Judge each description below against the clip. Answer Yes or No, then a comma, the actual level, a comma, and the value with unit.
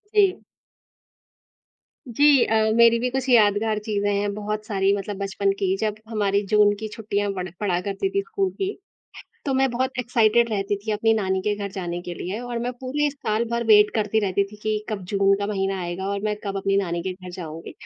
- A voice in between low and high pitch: No, high, 210 Hz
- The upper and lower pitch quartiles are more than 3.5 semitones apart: No, average, 2.9 semitones